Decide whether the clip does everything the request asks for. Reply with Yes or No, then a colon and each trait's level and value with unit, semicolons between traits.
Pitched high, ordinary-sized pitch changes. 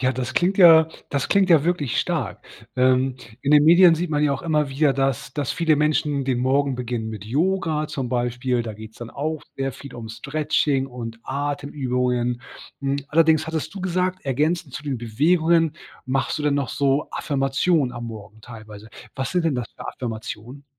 No: medium, 140 Hz; average, 4.0 semitones